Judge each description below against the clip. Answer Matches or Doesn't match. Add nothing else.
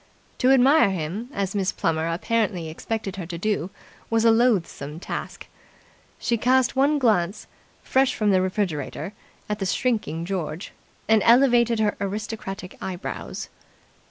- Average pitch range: Matches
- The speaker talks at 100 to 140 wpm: Matches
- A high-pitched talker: Matches